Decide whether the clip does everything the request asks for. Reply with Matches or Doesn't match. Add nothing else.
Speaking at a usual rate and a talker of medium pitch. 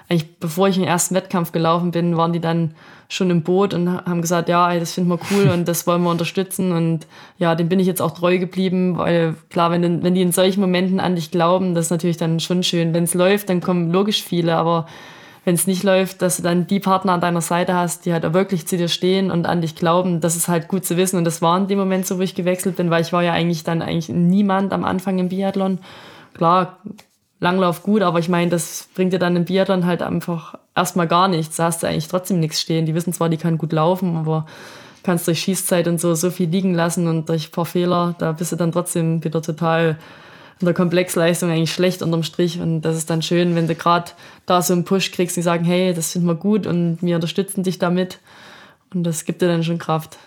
Doesn't match